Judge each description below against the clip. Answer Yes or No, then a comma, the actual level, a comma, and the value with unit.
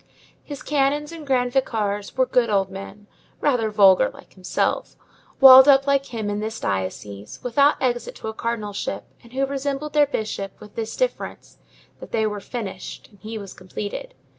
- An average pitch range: Yes, average, 4.9 semitones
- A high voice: Yes, high, 230 Hz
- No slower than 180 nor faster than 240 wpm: No, average, 170 wpm